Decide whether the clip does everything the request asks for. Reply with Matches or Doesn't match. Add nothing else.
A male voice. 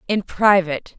Doesn't match